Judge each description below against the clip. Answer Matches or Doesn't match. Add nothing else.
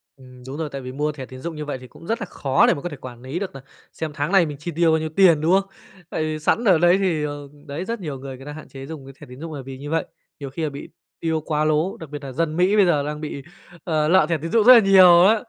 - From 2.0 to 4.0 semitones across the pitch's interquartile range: Matches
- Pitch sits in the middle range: Matches